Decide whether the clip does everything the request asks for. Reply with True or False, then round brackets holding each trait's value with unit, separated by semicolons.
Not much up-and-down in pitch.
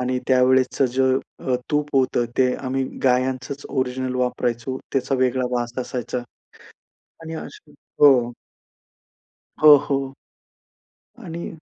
True (1.2 semitones)